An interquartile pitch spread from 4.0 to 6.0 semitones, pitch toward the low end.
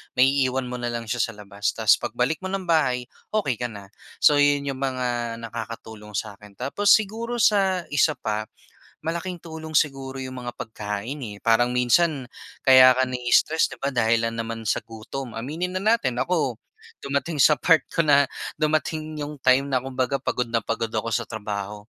Yes: average, 4.8 semitones; low, 130 Hz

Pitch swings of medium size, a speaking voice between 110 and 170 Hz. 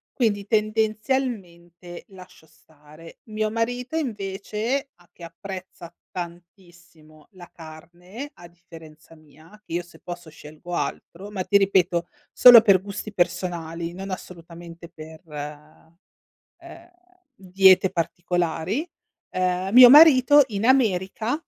No: average, 4.2 semitones; medium, 180 Hz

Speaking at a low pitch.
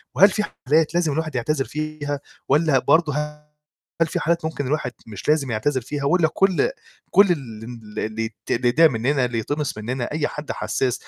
No: medium, 145 Hz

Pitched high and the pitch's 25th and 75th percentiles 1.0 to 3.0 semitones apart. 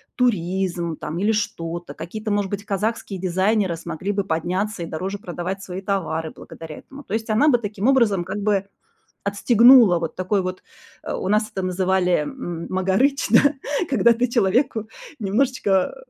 No: high, 195 Hz; average, 3.4 semitones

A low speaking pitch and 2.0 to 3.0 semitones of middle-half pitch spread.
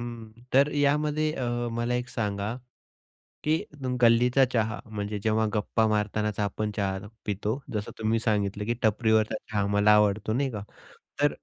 Yes: low, 110 Hz; narrow, 2.6 semitones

